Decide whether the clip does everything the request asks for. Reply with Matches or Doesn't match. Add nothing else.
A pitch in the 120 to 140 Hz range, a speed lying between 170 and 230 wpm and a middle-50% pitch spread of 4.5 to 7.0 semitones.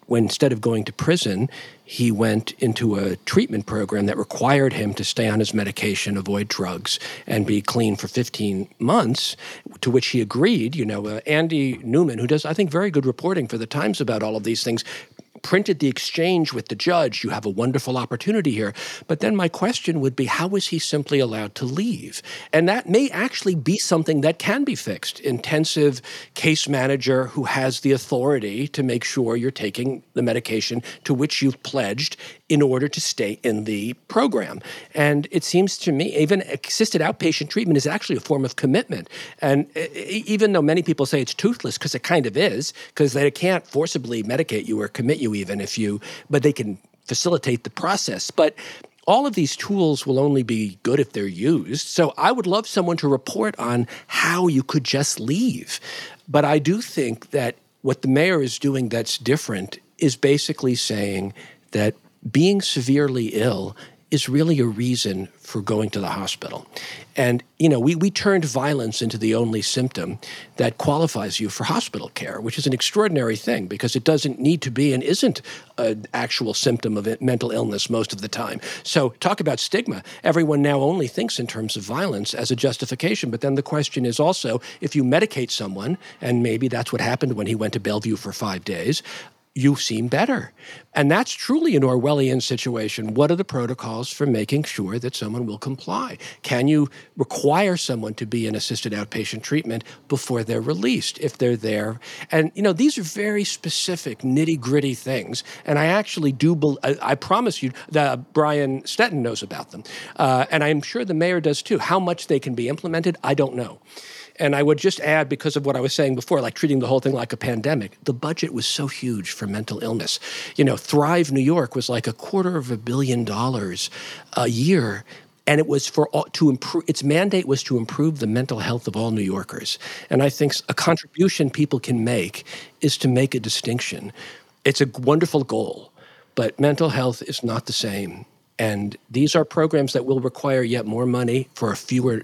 Matches